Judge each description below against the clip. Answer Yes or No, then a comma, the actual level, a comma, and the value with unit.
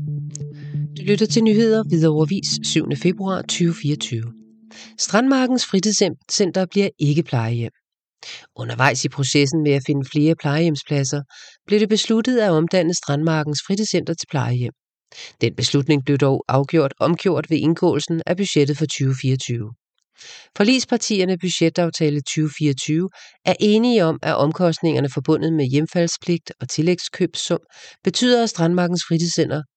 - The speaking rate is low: Yes, slow, 120 wpm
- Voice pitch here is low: No, medium, 160 Hz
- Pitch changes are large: No, average, 4.3 semitones